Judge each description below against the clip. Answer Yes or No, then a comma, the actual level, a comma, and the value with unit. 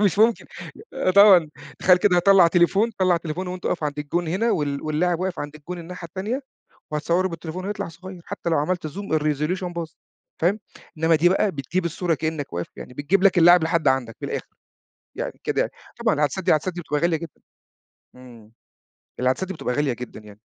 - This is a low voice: No, medium, 170 Hz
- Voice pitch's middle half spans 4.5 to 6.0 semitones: No, average, 3.6 semitones